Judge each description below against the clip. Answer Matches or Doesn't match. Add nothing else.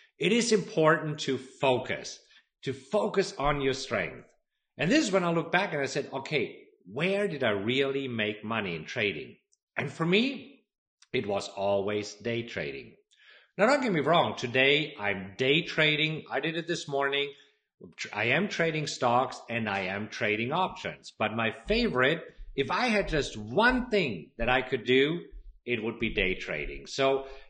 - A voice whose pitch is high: Doesn't match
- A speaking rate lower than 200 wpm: Matches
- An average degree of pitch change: Doesn't match